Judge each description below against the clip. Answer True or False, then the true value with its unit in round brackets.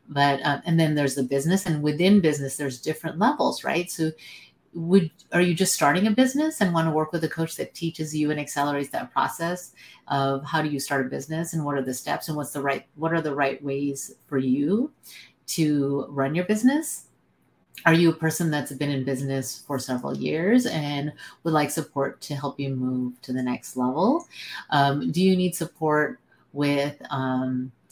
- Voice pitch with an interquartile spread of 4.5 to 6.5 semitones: False (3.3 semitones)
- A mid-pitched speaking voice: True (150 Hz)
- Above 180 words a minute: True (200 wpm)